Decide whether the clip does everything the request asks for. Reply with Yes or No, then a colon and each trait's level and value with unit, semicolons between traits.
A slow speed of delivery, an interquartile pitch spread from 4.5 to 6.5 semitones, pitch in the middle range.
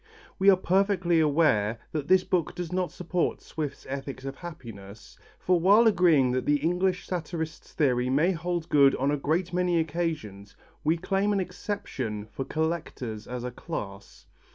No: average, 160 wpm; average, 5.2 semitones; medium, 160 Hz